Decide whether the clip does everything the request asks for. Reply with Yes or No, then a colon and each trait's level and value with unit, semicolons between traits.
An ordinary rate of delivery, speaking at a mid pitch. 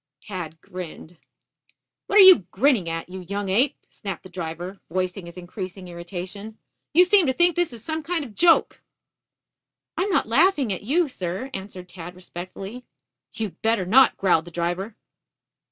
No: average, 170 wpm; high, 195 Hz